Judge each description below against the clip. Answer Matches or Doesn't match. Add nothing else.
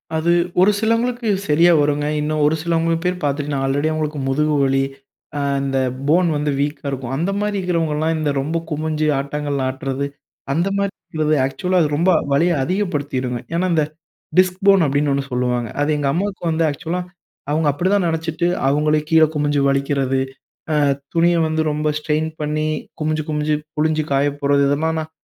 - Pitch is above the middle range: Doesn't match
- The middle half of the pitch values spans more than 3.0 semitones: Doesn't match